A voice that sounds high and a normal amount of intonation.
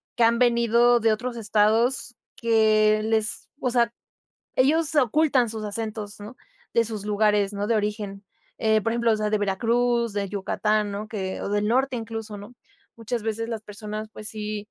No: high, 220 Hz; narrow, 2.0 semitones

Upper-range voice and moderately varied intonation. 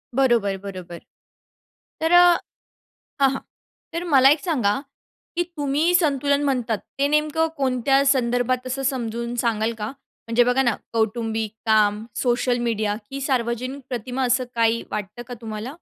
Yes: high, 245 Hz; average, 3.4 semitones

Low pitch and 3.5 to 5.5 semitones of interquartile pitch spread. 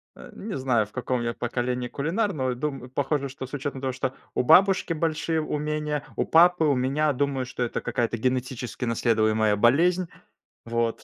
Yes: low, 130 Hz; average, 3.8 semitones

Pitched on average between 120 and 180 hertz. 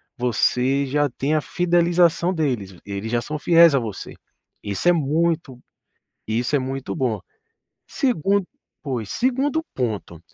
Yes: medium, 140 Hz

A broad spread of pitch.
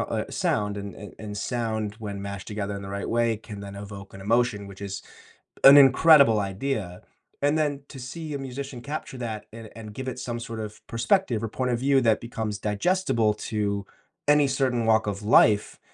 No: average, 4.2 semitones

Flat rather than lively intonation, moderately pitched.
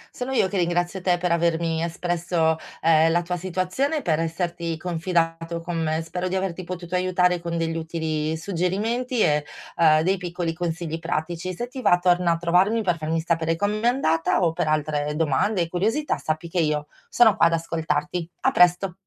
Yes: narrow, 2.0 semitones; medium, 170 Hz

